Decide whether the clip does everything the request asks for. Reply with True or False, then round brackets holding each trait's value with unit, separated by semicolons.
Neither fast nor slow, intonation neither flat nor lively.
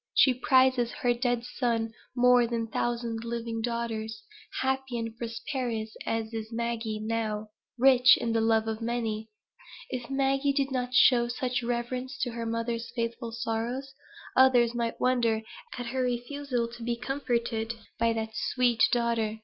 False (150 wpm; 1.7 semitones)